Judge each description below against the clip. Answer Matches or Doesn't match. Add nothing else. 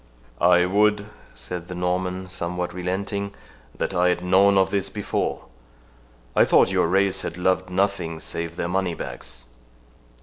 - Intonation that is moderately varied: Doesn't match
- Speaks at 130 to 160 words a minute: Matches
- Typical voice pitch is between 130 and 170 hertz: Doesn't match